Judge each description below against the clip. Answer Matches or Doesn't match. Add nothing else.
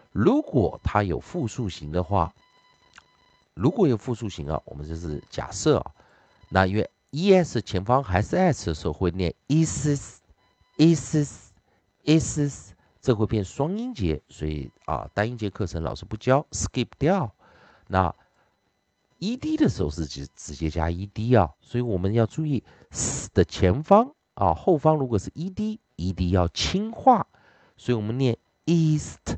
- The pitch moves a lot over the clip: Matches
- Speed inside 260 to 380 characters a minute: Doesn't match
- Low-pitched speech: Matches